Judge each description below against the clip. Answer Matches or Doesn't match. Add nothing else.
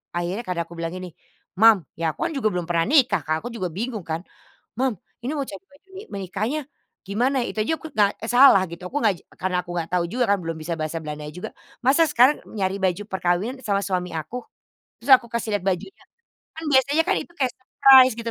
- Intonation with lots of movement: Matches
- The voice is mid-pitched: Doesn't match